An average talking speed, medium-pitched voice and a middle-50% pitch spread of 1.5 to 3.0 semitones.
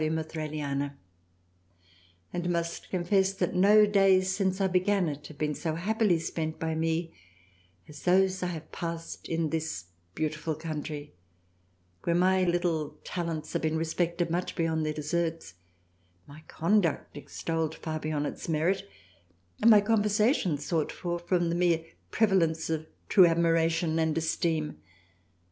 Yes: average, 145 wpm; medium, 165 Hz; narrow, 2.6 semitones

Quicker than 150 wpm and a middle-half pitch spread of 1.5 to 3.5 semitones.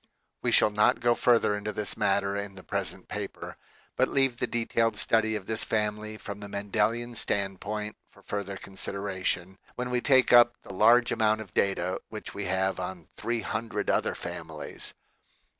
Yes: average, 170 wpm; narrow, 2.6 semitones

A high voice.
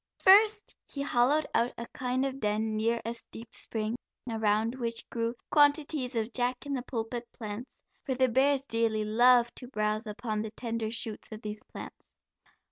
Yes: high, 235 Hz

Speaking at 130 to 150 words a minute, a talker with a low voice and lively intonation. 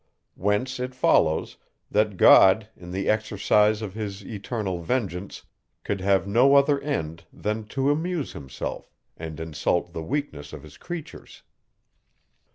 Yes: slow, 135 wpm; low, 105 Hz; wide, 6.3 semitones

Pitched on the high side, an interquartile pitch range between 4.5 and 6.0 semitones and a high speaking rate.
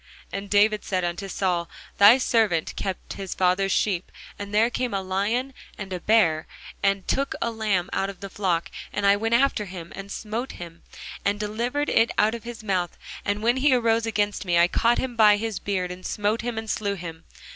No: high, 205 Hz; average, 3.2 semitones; fast, 210 wpm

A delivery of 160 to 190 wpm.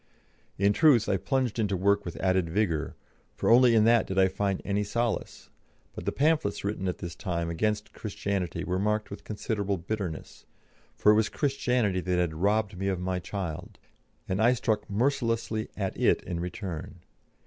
Yes: average, 175 wpm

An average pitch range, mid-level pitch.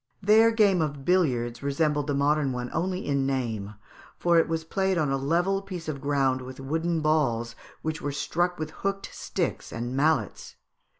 Yes: average, 4.4 semitones; medium, 150 Hz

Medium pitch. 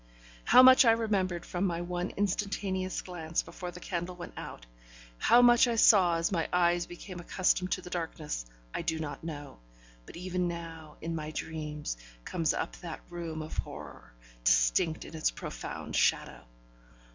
Yes: medium, 175 Hz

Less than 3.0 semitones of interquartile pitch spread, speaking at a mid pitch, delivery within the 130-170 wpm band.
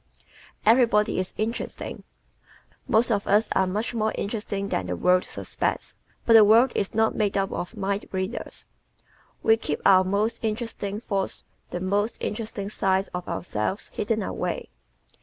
No: narrow, 2.5 semitones; high, 205 Hz; average, 160 wpm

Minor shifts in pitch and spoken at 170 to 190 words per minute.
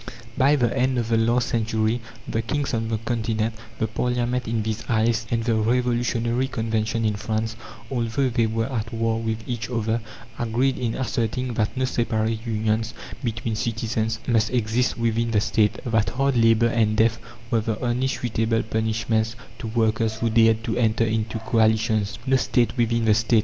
Yes: narrow, 1.3 semitones; average, 175 wpm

